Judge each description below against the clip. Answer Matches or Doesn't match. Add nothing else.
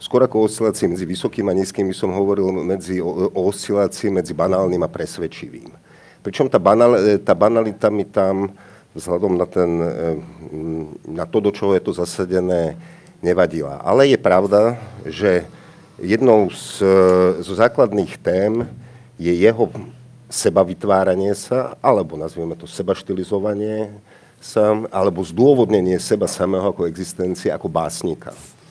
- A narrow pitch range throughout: Doesn't match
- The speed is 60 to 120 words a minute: Doesn't match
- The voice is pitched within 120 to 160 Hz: Doesn't match